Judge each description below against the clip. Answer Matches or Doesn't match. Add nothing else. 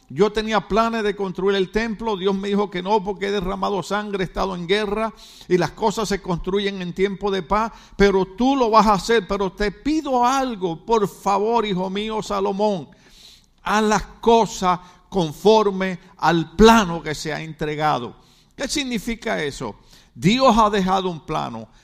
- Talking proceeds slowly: Doesn't match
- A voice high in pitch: Matches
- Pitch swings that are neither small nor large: Matches